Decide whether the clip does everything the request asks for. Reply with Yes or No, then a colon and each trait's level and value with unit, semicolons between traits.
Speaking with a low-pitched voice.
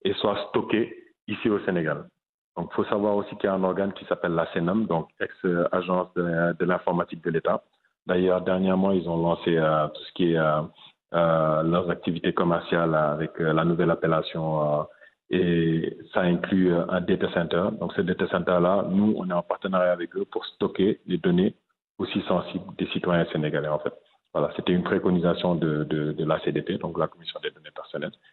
Yes: very low, 85 Hz